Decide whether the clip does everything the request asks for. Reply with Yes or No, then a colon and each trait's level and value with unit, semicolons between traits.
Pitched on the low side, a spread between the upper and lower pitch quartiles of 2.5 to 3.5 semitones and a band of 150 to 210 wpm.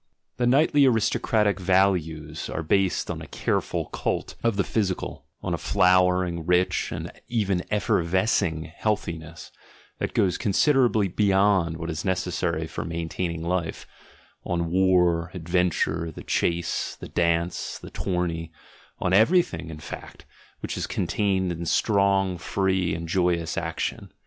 No: very low, 90 Hz; average, 2.8 semitones; slow, 135 wpm